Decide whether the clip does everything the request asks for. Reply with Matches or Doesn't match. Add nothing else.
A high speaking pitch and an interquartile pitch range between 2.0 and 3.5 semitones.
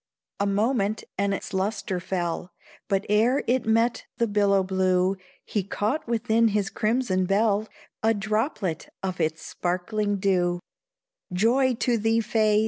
Matches